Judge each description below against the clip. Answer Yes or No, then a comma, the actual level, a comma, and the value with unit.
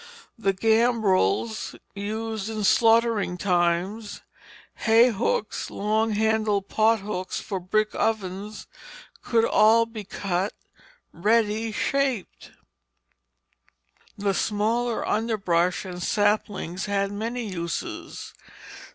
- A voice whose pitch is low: No, high, 210 Hz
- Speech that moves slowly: Yes, slow, 90 wpm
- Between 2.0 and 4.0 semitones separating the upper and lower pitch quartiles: Yes, narrow, 2.4 semitones